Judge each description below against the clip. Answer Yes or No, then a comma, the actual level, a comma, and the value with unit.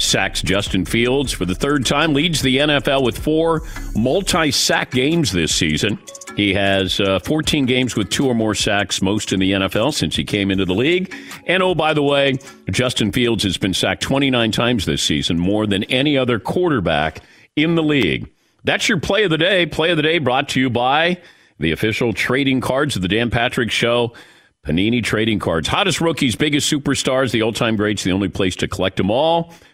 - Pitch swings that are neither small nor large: No, wide, 6.3 semitones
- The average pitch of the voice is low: Yes, low, 120 Hz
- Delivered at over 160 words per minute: Yes, average, 200 wpm